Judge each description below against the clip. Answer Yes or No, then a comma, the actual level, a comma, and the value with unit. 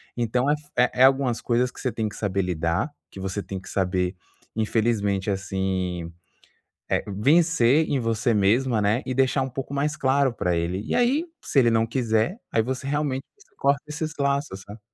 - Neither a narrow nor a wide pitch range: No, wide, 5.8 semitones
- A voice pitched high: No, low, 115 Hz